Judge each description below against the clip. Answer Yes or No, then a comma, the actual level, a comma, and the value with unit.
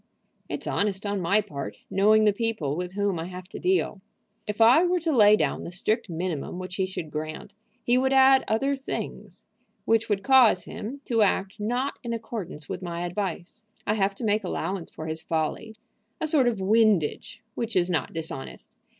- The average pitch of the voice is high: Yes, high, 205 Hz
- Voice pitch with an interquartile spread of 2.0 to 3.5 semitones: No, average, 4.3 semitones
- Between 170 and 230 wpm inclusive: Yes, average, 190 wpm